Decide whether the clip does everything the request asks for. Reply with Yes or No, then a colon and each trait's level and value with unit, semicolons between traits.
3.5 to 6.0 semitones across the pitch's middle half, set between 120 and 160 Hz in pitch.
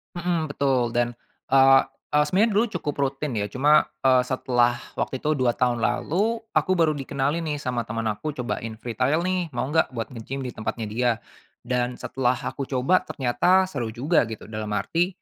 Yes: average, 4.1 semitones; low, 135 Hz